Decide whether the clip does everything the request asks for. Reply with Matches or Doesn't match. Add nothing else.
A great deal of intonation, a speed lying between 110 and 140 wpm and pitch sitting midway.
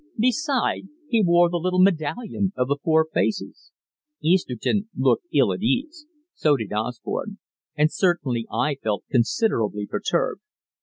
Matches